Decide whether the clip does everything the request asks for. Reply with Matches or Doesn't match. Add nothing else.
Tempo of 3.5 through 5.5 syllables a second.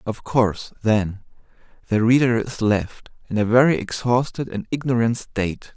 Matches